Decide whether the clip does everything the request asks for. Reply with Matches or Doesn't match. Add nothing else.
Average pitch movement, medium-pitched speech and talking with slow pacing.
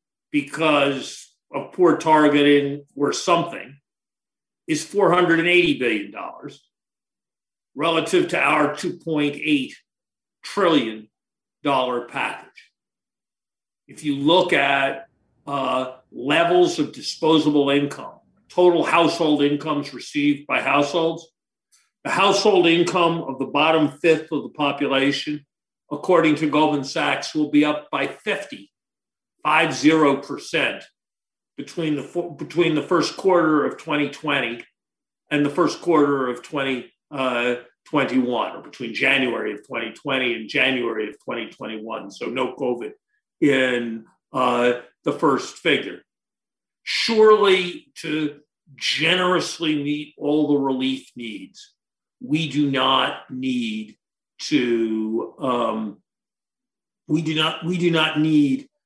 Matches